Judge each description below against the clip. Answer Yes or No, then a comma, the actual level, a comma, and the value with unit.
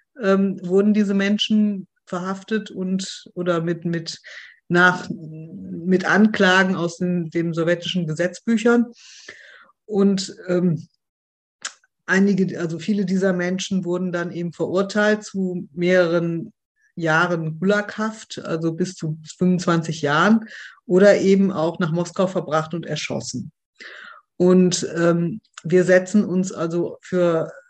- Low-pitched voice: No, medium, 180 Hz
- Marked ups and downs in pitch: No, narrow, 2.6 semitones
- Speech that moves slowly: Yes, slow, 115 wpm